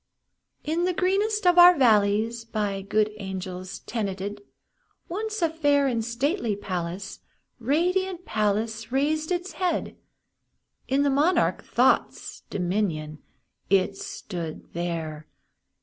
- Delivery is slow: Yes, slow, 110 wpm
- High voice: Yes, high, 225 Hz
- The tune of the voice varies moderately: No, wide, 8.9 semitones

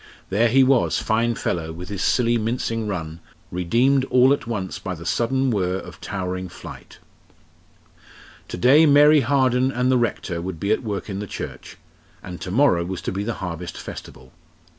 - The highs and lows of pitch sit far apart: Yes, wide, 5.8 semitones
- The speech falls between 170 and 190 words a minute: Yes, average, 180 wpm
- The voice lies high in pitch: No, low, 110 Hz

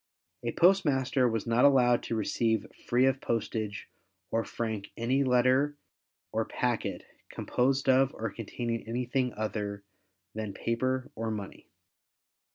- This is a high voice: No, low, 120 Hz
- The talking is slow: Yes, slow, 125 wpm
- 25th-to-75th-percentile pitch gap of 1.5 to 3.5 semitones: Yes, average, 2.8 semitones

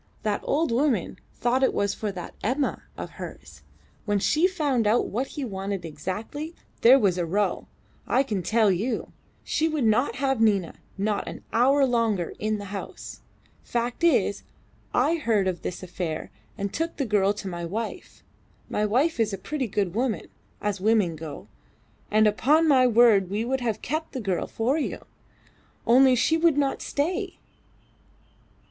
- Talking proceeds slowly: No, average, 165 wpm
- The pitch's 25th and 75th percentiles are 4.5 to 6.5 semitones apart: Yes, average, 5.1 semitones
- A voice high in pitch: Yes, high, 225 Hz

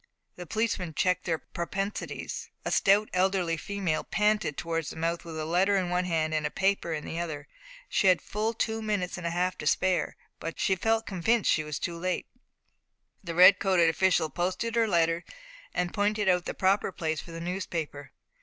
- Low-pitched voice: No, medium, 180 Hz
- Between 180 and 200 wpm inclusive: Yes, average, 190 wpm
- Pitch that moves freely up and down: No, average, 3.0 semitones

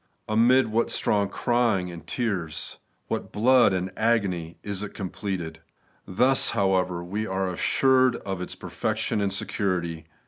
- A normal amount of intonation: Yes, average, 4.1 semitones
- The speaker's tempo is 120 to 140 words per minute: Yes, slow, 135 wpm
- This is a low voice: Yes, low, 100 Hz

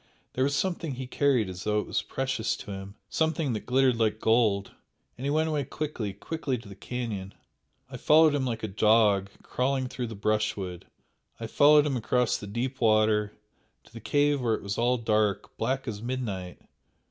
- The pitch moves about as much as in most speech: Yes, average, 4.0 semitones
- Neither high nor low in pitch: No, low, 115 Hz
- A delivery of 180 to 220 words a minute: Yes, average, 190 wpm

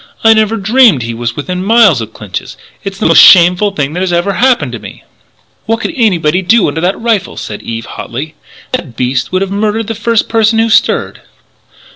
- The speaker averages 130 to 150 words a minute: No, average, 200 wpm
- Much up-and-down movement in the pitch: Yes, wide, 6.7 semitones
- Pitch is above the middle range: Yes, high, 195 Hz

